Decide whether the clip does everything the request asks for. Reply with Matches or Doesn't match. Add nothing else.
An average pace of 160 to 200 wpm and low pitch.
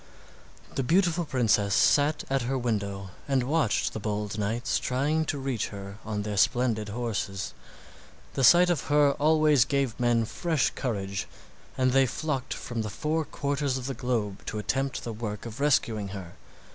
Matches